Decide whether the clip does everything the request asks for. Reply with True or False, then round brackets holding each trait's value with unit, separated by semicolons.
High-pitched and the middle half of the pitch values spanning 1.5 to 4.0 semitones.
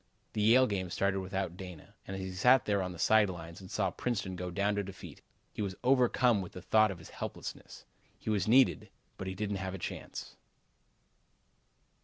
False (95 Hz; 2.7 semitones)